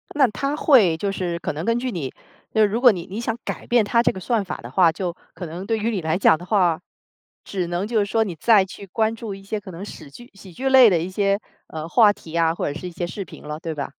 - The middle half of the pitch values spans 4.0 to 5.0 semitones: Yes, average, 4.7 semitones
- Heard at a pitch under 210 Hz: Yes, high, 195 Hz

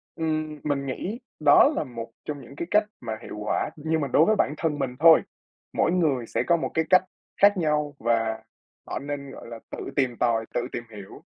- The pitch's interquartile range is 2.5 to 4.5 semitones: No, average, 5.2 semitones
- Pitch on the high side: No, medium, 145 Hz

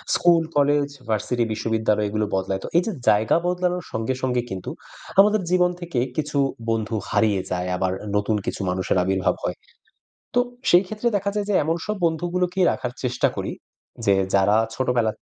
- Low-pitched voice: Yes, low, 125 Hz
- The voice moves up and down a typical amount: No, wide, 8.8 semitones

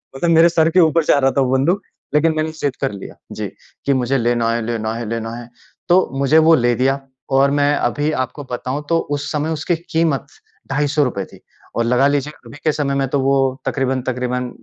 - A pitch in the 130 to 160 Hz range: Yes, medium, 140 Hz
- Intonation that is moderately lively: Yes, average, 3.2 semitones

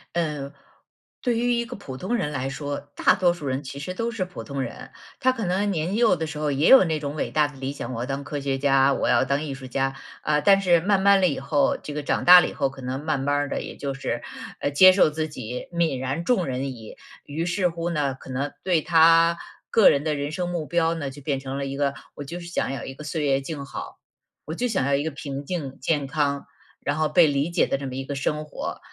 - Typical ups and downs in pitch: Yes, average, 3.9 semitones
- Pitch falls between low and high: Yes, medium, 150 Hz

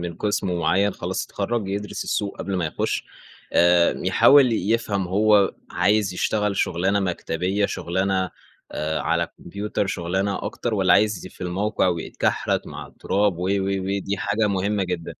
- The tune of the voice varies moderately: No, narrow, 2.3 semitones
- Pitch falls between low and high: No, very low, 95 Hz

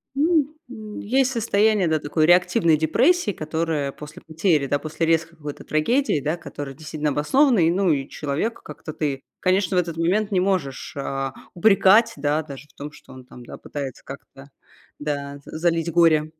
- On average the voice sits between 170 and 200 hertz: No, medium, 160 Hz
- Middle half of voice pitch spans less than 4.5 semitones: No, average, 5.0 semitones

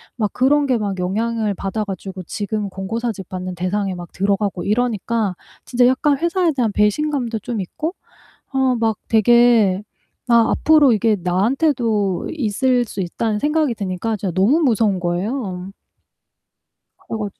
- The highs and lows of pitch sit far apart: No, average, 4.2 semitones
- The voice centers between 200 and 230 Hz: Yes, high, 220 Hz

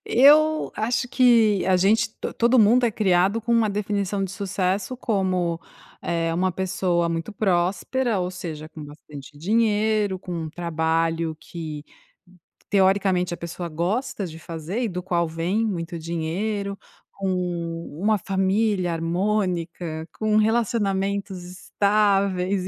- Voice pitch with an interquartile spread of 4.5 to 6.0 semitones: No, average, 3.8 semitones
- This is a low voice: No, high, 190 Hz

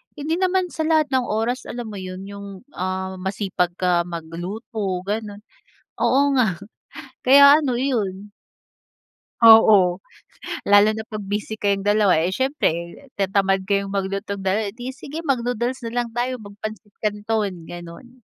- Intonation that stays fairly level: No, average, 4.2 semitones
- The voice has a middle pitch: No, high, 210 Hz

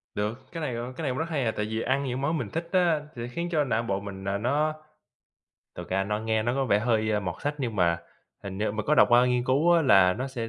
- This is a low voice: Yes, low, 120 Hz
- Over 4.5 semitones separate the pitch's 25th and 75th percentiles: Yes, average, 5.2 semitones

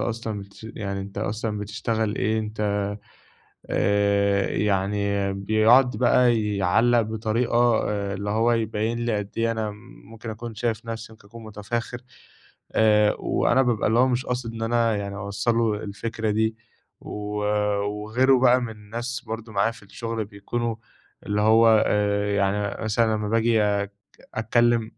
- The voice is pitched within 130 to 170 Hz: No, low, 110 Hz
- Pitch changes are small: Yes, narrow, 2.1 semitones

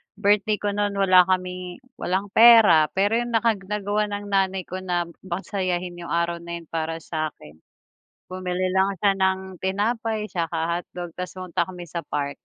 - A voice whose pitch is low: No, medium, 185 Hz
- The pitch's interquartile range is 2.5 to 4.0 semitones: Yes, average, 2.8 semitones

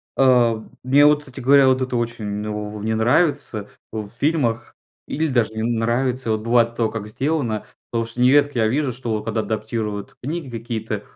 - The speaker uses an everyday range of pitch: Yes, average, 3.2 semitones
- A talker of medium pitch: No, low, 115 Hz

